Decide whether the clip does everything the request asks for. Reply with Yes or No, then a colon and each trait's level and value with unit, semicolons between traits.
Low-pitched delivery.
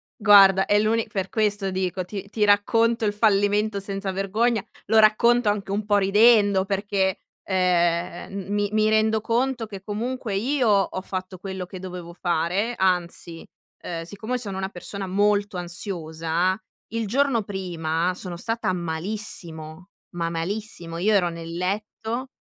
No: high, 195 Hz